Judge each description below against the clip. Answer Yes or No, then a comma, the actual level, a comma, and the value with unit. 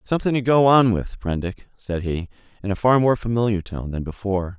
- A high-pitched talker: No, low, 105 Hz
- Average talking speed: No, fast, 210 wpm